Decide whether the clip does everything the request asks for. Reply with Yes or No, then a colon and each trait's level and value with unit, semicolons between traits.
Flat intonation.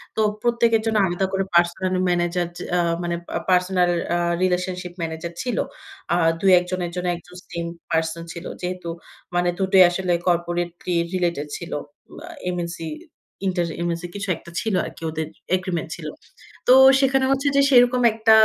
Yes: narrow, 1.9 semitones